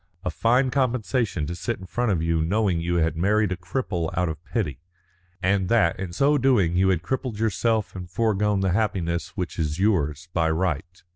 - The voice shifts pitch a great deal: No, average, 4.7 semitones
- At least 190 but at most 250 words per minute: Yes, average, 195 wpm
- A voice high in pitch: No, very low, 95 Hz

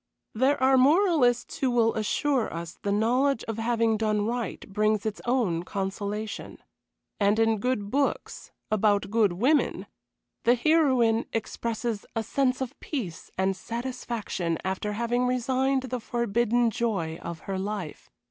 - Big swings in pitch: No, average, 3.5 semitones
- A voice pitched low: No, high, 225 Hz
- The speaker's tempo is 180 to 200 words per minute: No, average, 140 wpm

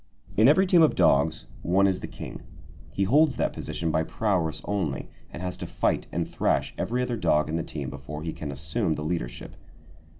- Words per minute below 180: No, average, 200 wpm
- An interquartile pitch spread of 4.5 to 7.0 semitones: Yes, average, 5.0 semitones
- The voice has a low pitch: Yes, very low, 85 Hz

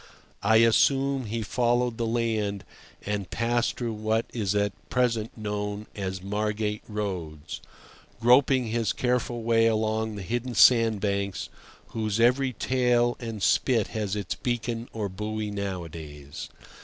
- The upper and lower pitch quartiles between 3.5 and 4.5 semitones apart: No, average, 2.7 semitones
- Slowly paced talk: Yes, slow, 130 wpm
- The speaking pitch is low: Yes, low, 110 Hz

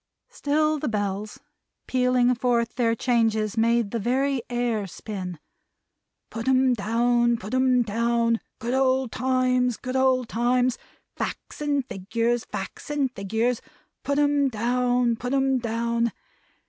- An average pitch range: No, narrow, 2.1 semitones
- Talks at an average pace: No, slow, 130 wpm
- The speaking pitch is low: No, high, 240 Hz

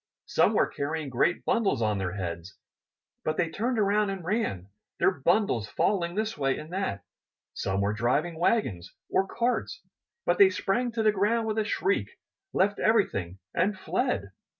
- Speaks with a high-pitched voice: No, medium, 175 Hz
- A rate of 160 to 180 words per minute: Yes, average, 165 wpm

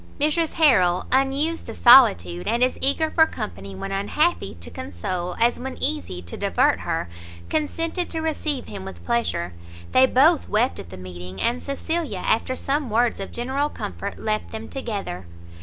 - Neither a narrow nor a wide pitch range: No, wide, 8.7 semitones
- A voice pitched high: Yes, high, 240 Hz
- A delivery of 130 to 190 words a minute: Yes, average, 165 wpm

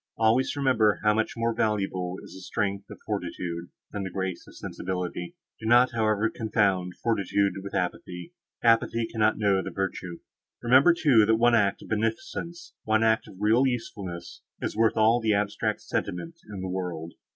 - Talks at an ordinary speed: Yes, average, 170 wpm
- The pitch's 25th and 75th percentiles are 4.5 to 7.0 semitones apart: No, average, 3.3 semitones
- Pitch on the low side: Yes, low, 105 Hz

